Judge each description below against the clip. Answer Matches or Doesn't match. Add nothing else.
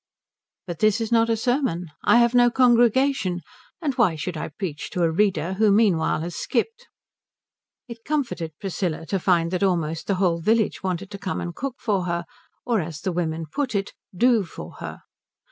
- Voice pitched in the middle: Doesn't match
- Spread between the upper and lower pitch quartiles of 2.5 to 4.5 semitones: Doesn't match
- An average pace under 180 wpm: Doesn't match